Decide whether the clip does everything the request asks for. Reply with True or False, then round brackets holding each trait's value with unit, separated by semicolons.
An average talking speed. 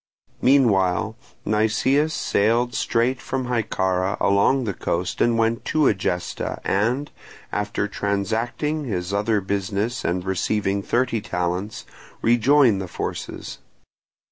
False (110 wpm)